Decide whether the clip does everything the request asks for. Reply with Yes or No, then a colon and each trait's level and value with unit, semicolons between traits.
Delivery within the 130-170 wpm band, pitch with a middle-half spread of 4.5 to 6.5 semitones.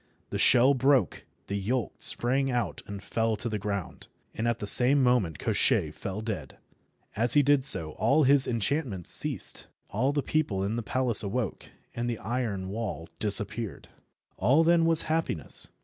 Yes: average, 165 wpm; average, 4.9 semitones